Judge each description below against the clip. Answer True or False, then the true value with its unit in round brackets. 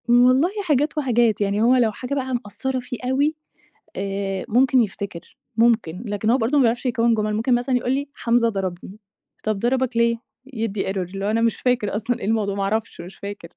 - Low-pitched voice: False (230 Hz)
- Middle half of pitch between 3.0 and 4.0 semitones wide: True (3.7 semitones)